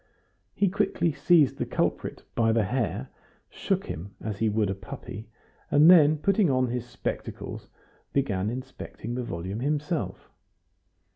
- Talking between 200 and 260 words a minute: No, average, 140 wpm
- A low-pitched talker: Yes, low, 125 Hz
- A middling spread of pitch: No, wide, 5.7 semitones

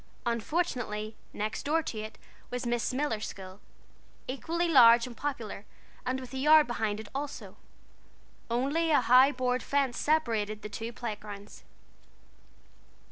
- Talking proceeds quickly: No, slow, 135 wpm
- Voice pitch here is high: Yes, high, 245 Hz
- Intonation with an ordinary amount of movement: Yes, average, 4.7 semitones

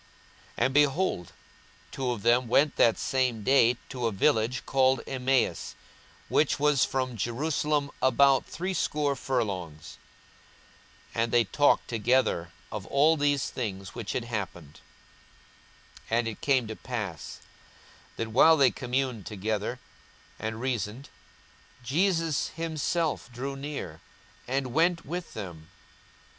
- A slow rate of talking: Yes, slow, 125 wpm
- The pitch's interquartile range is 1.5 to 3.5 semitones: No, average, 4.2 semitones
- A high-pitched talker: No, low, 130 Hz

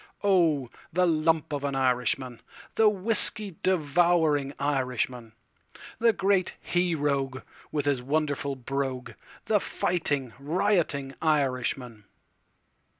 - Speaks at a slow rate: Yes, slow, 90 wpm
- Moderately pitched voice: Yes, medium, 145 Hz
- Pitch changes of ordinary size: Yes, average, 5.0 semitones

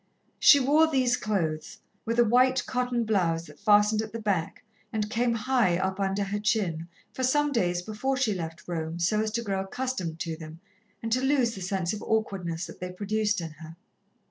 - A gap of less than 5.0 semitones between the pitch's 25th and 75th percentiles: No, average, 5.3 semitones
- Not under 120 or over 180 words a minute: No, average, 195 wpm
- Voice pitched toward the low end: No, high, 210 Hz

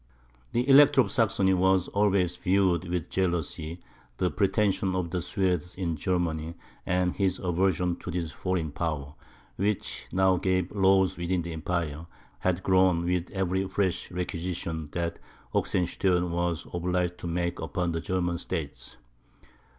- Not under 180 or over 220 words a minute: No, average, 140 wpm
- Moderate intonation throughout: No, narrow, 1.7 semitones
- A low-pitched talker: Yes, very low, 90 Hz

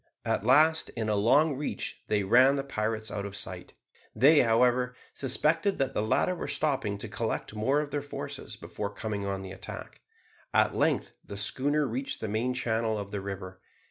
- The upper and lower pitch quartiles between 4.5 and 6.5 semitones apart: Yes, average, 4.9 semitones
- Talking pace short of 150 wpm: No, average, 190 wpm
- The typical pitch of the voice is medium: No, low, 115 Hz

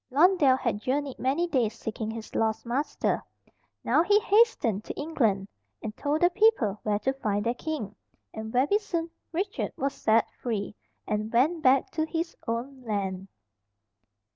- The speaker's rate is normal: Yes, average, 155 wpm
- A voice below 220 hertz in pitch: No, very high, 260 Hz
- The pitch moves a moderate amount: No, wide, 6.7 semitones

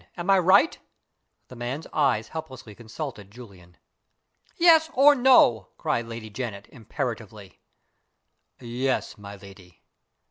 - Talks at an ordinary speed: No, slow, 110 wpm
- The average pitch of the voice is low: Yes, low, 120 Hz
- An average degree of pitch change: No, wide, 7.4 semitones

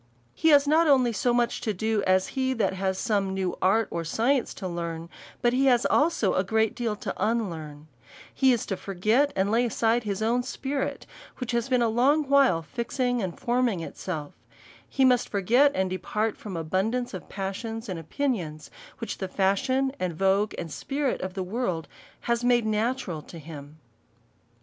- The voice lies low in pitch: No, high, 220 Hz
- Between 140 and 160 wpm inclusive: No, average, 185 wpm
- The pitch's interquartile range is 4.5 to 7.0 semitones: Yes, average, 4.9 semitones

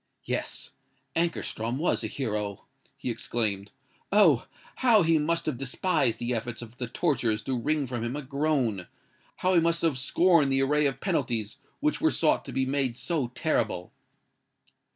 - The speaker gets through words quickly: No, average, 155 wpm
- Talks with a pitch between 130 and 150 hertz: Yes, low, 135 Hz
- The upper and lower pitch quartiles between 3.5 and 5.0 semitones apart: No, wide, 5.4 semitones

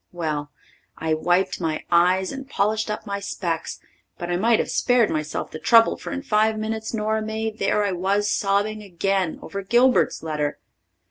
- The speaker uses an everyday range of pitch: Yes, average, 4.0 semitones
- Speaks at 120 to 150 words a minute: No, average, 175 wpm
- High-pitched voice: Yes, high, 200 Hz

